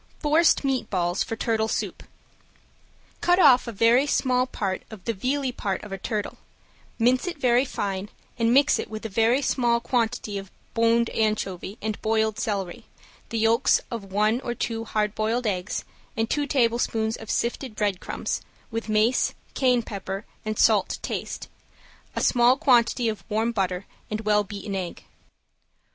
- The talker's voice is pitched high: Yes, high, 225 Hz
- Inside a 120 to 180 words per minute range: Yes, average, 160 wpm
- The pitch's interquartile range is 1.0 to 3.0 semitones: Yes, average, 2.7 semitones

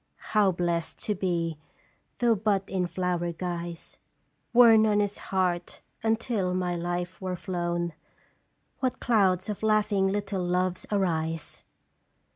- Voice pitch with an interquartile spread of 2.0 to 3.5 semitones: Yes, average, 3.0 semitones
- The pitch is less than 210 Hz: Yes, medium, 185 Hz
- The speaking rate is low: Yes, slow, 125 wpm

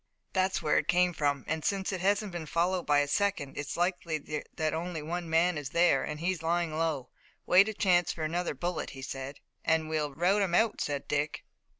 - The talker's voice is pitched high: No, medium, 165 Hz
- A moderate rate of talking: No, fast, 215 wpm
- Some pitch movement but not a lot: Yes, average, 3.1 semitones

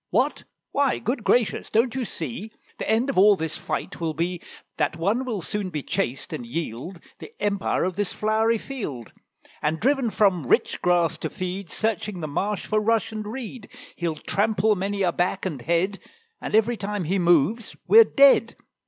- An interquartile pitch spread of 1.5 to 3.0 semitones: No, average, 4.5 semitones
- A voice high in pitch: Yes, high, 200 Hz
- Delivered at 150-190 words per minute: Yes, average, 180 wpm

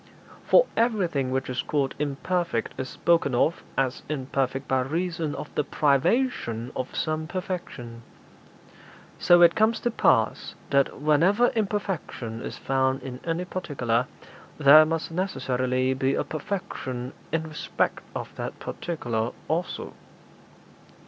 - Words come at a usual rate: No, slow, 125 wpm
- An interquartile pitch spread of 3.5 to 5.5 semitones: Yes, average, 5.1 semitones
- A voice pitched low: No, medium, 150 Hz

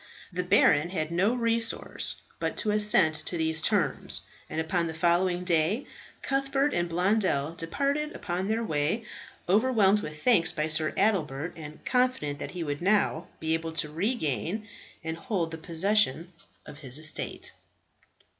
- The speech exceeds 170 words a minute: No, average, 150 wpm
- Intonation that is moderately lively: Yes, average, 5.0 semitones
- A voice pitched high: No, medium, 175 Hz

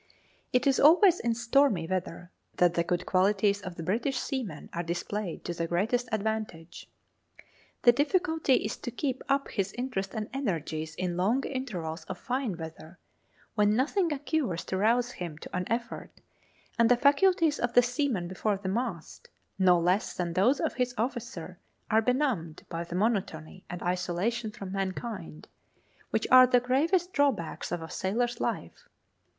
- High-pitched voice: Yes, high, 215 Hz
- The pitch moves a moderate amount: No, wide, 6.0 semitones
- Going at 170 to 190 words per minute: No, average, 160 wpm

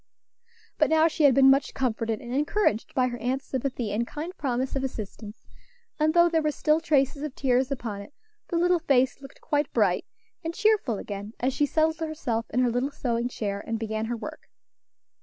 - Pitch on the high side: Yes, very high, 265 Hz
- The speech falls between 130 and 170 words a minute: No, average, 195 wpm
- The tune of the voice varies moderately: Yes, average, 4.7 semitones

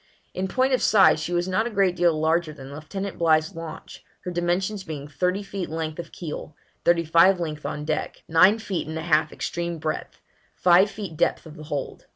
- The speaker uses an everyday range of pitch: Yes, average, 3.2 semitones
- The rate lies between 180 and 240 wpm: Yes, fast, 205 wpm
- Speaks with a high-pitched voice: No, medium, 170 Hz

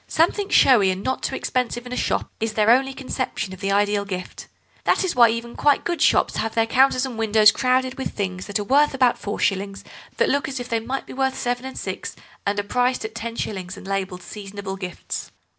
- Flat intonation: No, average, 4.3 semitones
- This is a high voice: Yes, high, 230 Hz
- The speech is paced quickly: Yes, fast, 220 wpm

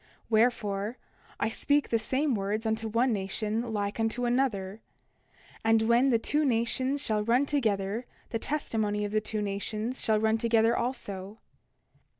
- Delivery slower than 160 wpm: Yes, average, 150 wpm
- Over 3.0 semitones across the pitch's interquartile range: No, narrow, 2.5 semitones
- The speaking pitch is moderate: No, high, 225 Hz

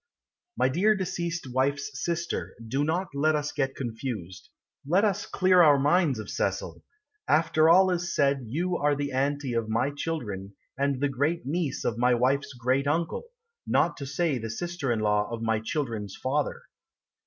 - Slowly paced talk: No, average, 170 wpm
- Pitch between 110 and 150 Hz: Yes, medium, 140 Hz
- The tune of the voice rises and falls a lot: No, average, 5.0 semitones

